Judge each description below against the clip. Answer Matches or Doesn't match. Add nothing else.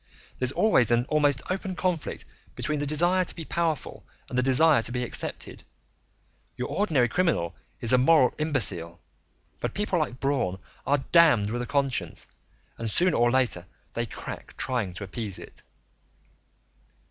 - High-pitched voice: Doesn't match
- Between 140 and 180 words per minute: Matches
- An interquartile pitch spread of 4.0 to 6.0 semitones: Matches